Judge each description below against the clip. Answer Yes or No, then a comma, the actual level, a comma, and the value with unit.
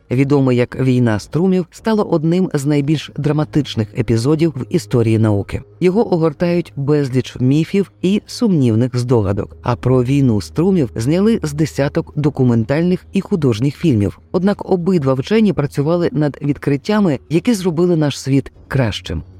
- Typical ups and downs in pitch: No, wide, 5.8 semitones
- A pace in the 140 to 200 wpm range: No, average, 130 wpm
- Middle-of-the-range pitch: Yes, medium, 145 Hz